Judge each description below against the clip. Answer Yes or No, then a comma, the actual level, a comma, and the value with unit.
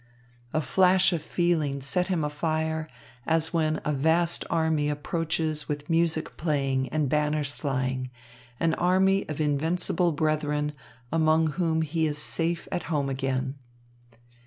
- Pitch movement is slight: Yes, narrow, 2.0 semitones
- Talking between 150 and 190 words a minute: No, slow, 135 wpm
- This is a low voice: No, medium, 155 Hz